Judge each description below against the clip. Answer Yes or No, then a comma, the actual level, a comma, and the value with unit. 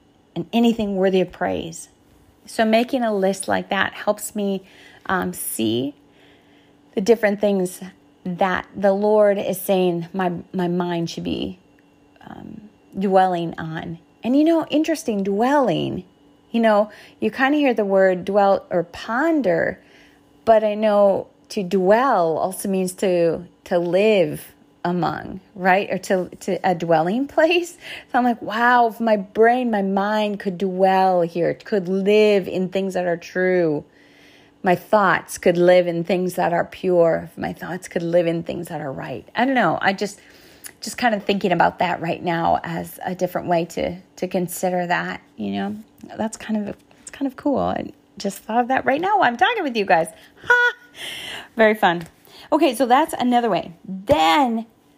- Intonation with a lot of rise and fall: No, average, 4.1 semitones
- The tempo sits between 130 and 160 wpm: No, average, 170 wpm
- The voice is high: Yes, high, 195 Hz